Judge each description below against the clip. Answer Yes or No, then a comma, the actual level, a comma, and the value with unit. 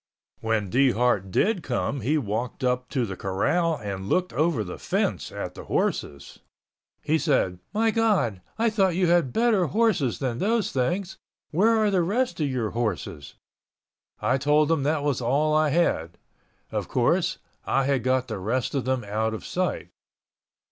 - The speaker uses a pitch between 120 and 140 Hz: Yes, low, 135 Hz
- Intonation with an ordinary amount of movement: No, wide, 7.5 semitones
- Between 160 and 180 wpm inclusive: Yes, average, 170 wpm